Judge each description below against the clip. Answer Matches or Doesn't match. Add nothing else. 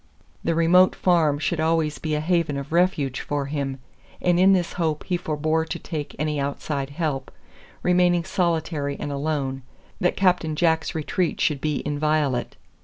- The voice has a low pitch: Doesn't match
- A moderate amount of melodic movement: Matches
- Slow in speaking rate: Doesn't match